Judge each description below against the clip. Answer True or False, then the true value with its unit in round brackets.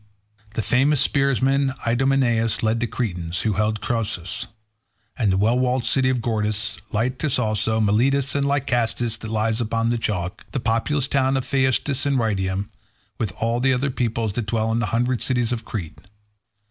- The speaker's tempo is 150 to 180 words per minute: True (165 wpm)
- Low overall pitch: True (115 Hz)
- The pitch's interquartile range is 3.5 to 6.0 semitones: False (3.1 semitones)